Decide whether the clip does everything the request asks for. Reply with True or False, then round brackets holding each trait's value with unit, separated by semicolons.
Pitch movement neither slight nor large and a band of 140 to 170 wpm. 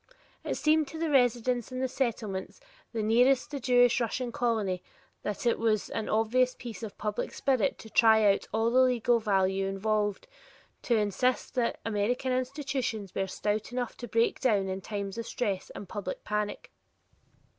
True (3.4 semitones; 165 wpm)